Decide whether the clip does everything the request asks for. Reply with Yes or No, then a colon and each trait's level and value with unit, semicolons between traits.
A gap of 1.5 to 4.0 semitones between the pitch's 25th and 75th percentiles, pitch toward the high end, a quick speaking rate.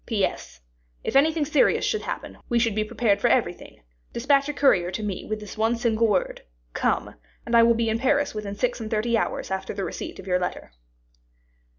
Yes: average, 3.6 semitones; high, 225 Hz; fast, 210 wpm